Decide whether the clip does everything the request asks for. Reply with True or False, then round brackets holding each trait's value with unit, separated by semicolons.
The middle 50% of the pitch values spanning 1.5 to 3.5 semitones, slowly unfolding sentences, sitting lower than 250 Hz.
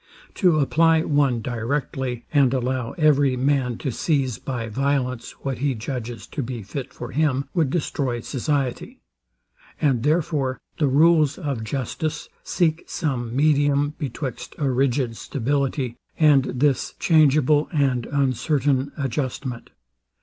True (2.9 semitones; 125 wpm; 135 Hz)